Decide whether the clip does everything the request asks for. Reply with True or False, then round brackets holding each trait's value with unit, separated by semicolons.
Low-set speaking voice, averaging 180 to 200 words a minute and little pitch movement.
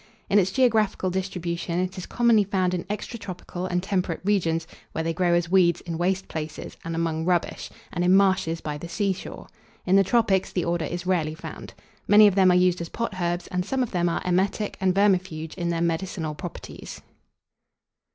False (180 Hz; 190 wpm; 2.1 semitones)